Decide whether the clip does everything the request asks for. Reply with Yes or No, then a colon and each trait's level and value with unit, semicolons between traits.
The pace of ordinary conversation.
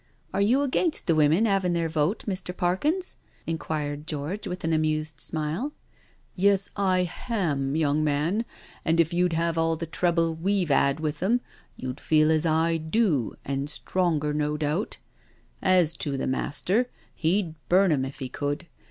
Yes: average, 170 wpm